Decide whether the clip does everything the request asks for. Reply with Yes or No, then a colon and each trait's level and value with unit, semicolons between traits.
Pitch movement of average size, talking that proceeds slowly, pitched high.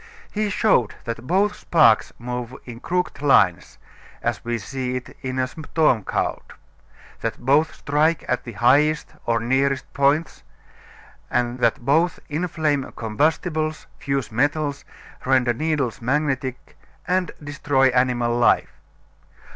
No: average, 4.1 semitones; slow, 115 wpm; low, 135 Hz